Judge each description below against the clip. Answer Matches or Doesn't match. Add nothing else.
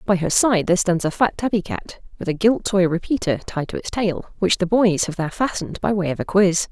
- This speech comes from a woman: Matches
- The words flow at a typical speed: Doesn't match